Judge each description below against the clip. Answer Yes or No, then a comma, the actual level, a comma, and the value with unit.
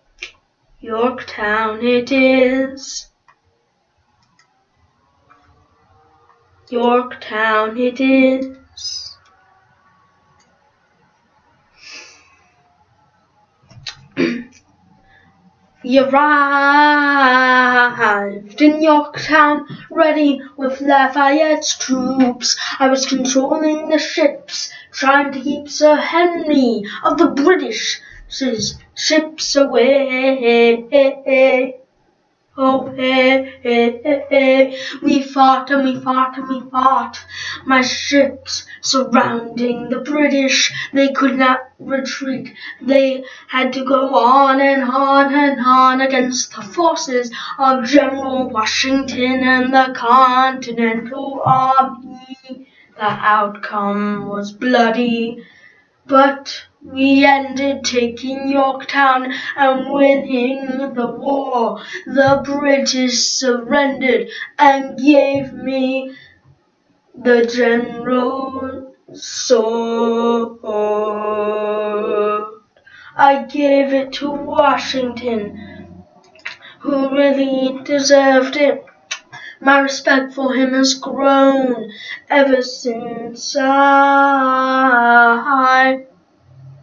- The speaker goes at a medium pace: No, slow, 75 wpm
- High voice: Yes, very high, 265 Hz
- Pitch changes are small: Yes, narrow, 2.0 semitones